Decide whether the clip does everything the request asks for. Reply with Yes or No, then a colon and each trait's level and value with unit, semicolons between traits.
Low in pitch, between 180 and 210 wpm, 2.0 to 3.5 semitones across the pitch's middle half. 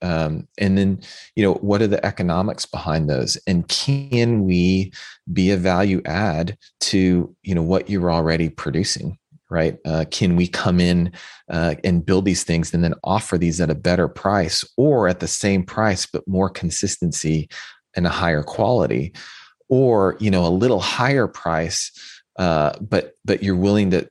No: very low, 90 Hz; average, 170 wpm; narrow, 2.5 semitones